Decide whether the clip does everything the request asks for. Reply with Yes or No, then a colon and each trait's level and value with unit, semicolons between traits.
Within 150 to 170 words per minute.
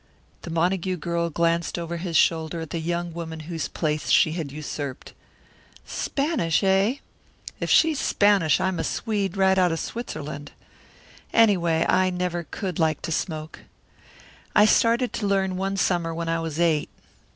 Yes: average, 160 wpm